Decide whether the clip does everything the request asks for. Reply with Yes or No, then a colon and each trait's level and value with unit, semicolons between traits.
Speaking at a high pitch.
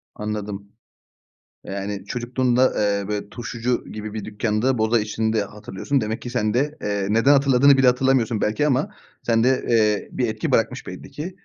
No: low, 115 Hz